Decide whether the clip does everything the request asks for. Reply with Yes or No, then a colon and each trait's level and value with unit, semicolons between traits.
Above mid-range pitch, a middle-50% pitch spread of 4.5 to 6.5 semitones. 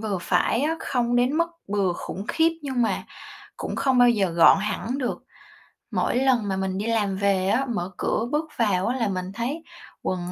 Yes: high, 220 Hz; average, 4.8 semitones